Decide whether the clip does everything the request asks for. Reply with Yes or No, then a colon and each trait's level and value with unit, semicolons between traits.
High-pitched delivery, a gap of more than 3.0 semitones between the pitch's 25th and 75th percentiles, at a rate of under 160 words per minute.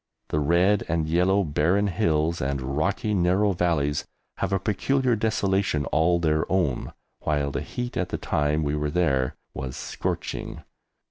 No: very low, 85 Hz; average, 4.7 semitones; average, 150 wpm